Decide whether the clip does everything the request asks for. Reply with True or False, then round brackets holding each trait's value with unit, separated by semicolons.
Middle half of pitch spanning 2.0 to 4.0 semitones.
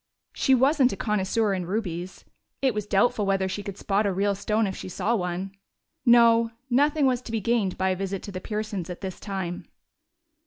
True (3.4 semitones)